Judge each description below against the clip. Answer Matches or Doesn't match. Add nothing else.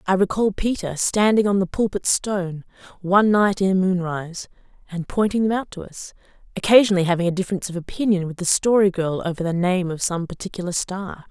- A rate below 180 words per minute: Doesn't match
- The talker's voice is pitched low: Doesn't match